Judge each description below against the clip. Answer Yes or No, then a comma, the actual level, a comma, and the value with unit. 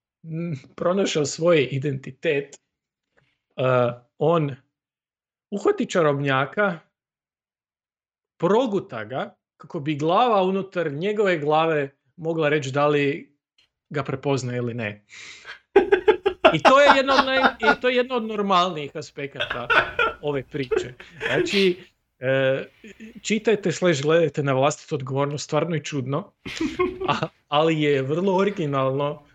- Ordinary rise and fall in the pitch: No, wide, 5.8 semitones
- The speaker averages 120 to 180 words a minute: No, slow, 110 wpm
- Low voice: No, medium, 155 Hz